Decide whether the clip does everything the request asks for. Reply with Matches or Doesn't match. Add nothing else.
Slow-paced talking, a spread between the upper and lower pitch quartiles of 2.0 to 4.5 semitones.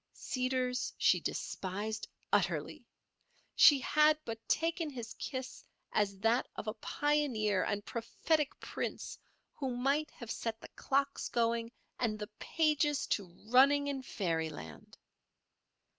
Doesn't match